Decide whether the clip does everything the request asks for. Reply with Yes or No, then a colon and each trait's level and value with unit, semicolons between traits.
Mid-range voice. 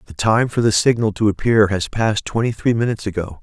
No: low, 105 Hz